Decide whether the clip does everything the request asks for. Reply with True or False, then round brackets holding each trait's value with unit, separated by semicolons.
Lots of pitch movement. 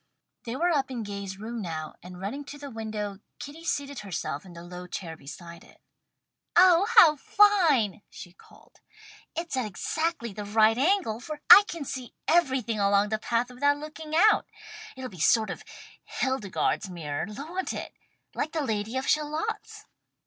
True (7.2 semitones)